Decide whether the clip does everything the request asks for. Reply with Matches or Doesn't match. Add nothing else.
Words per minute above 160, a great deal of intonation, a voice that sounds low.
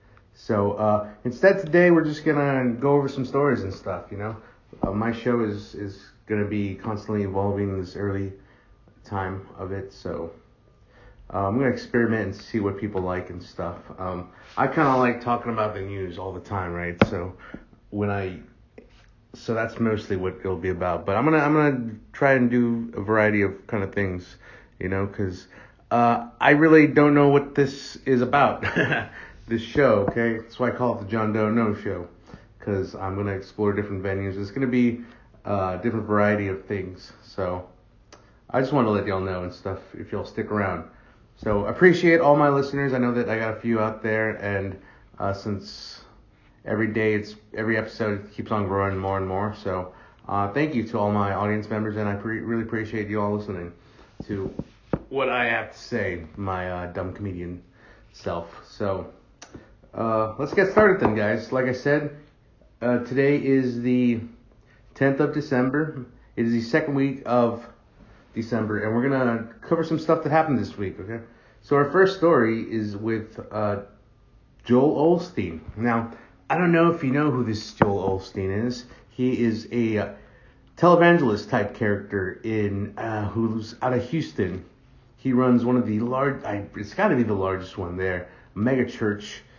Doesn't match